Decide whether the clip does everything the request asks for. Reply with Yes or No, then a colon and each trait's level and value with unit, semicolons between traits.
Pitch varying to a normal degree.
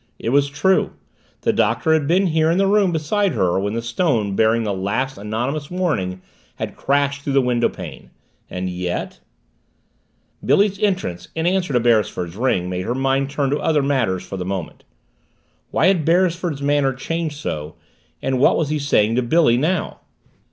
No: wide, 6.8 semitones